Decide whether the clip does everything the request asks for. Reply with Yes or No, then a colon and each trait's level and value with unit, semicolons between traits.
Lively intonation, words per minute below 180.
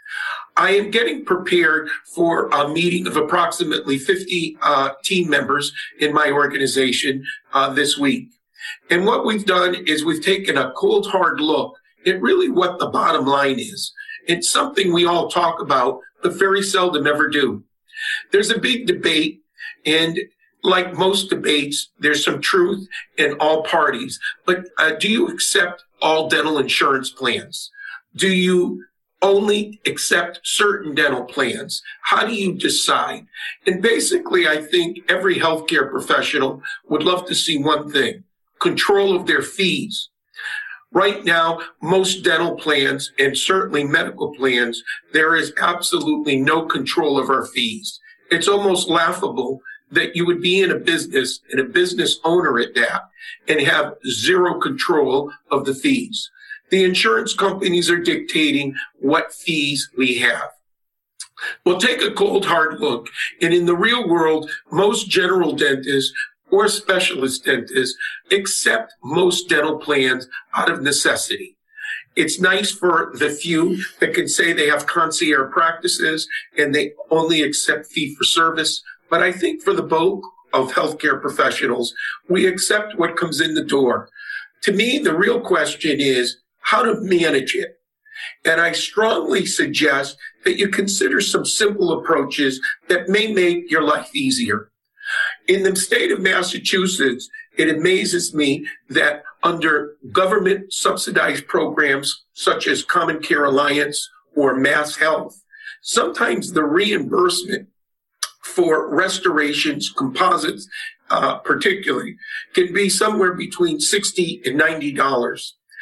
Yes: wide, 8.3 semitones; average, 140 wpm